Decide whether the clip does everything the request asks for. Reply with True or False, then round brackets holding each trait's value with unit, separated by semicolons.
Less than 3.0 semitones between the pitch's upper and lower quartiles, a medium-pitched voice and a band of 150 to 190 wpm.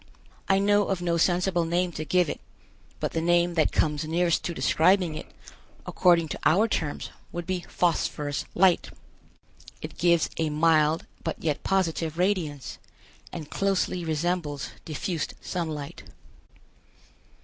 False (2.4 semitones; 170 Hz; 135 wpm)